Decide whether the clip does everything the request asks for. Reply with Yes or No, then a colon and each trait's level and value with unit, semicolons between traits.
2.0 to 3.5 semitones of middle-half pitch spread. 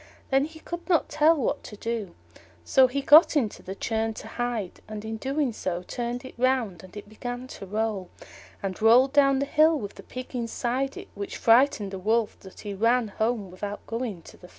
No: average, 4.4 semitones